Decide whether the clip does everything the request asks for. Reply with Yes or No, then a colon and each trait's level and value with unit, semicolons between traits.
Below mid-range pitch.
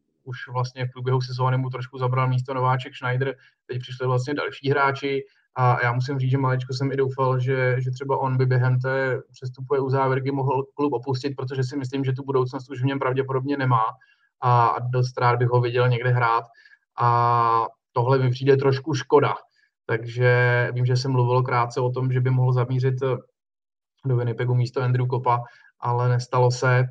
Yes: low, 130 Hz